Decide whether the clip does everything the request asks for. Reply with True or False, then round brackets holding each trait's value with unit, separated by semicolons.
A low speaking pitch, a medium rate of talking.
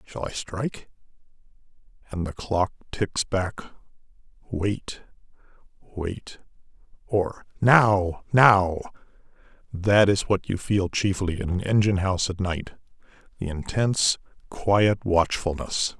False (95 Hz; 105 wpm)